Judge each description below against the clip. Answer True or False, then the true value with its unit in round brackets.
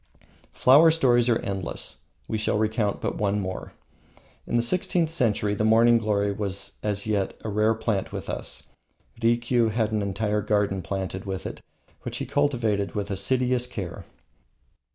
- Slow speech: False (155 wpm)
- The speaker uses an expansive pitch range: False (2.9 semitones)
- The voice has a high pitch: False (105 Hz)